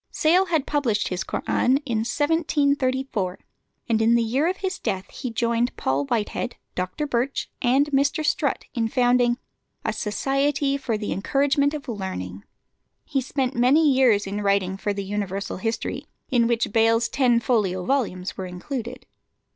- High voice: Yes, high, 240 Hz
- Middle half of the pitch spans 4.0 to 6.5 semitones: Yes, average, 5.0 semitones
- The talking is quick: No, average, 155 wpm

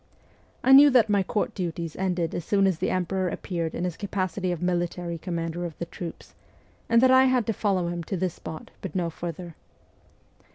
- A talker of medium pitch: Yes, medium, 180 Hz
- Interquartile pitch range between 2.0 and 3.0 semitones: Yes, average, 2.7 semitones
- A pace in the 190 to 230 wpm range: Yes, fast, 205 wpm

